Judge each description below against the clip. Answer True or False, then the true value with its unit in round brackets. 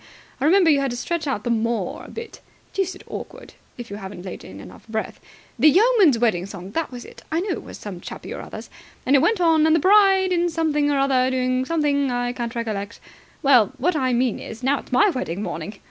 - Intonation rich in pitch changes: True (6.2 semitones)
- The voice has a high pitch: True (260 Hz)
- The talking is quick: True (235 wpm)